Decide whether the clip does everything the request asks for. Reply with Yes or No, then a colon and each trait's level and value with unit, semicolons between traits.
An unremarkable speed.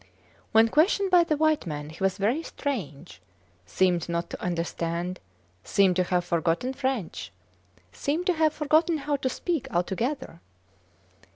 Yes: average, 145 wpm